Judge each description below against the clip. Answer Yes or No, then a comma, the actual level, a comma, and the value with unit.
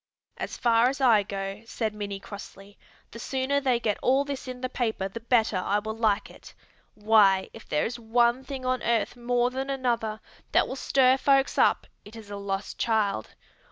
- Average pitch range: Yes, average, 3.6 semitones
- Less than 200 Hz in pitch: No, high, 230 Hz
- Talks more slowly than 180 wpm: No, average, 190 wpm